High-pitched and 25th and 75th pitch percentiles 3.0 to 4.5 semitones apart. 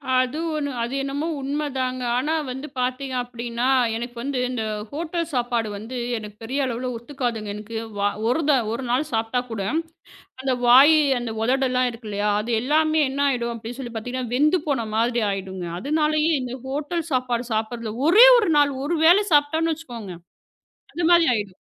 Yes: very high, 255 Hz; average, 3.8 semitones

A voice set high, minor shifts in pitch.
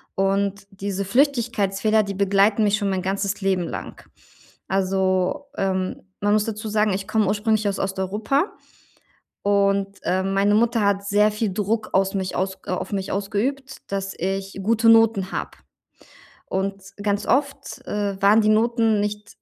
Yes: high, 200 Hz; narrow, 1.9 semitones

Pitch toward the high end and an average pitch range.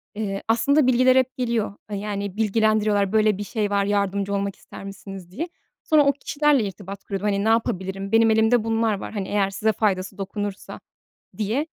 No: high, 210 Hz; narrow, 2.3 semitones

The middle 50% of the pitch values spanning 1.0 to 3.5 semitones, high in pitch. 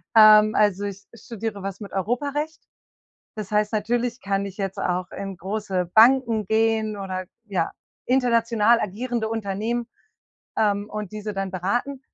Yes: average, 2.7 semitones; high, 215 Hz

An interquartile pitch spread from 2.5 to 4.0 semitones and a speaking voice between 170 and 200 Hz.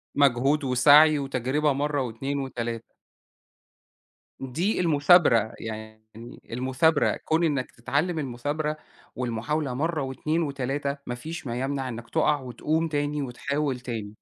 No: average, 3.5 semitones; medium, 140 Hz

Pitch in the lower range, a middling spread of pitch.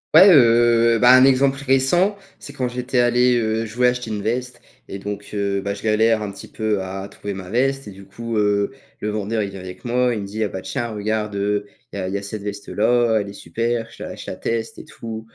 Yes: low, 110 Hz; average, 3.3 semitones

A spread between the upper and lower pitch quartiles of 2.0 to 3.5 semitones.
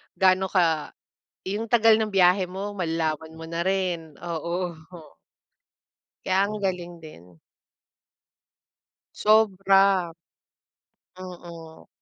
Yes: average, 2.8 semitones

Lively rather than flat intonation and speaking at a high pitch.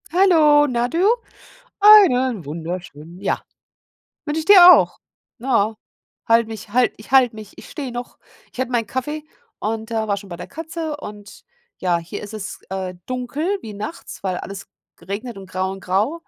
Yes: wide, 6.9 semitones; high, 230 Hz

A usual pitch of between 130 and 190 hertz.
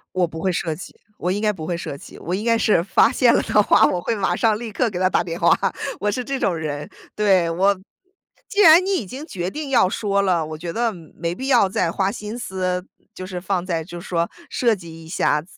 Yes: medium, 185 Hz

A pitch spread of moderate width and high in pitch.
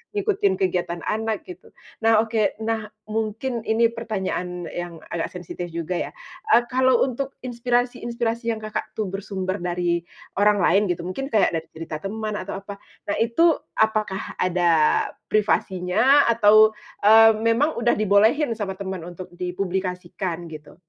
Yes: average, 4.1 semitones; high, 210 Hz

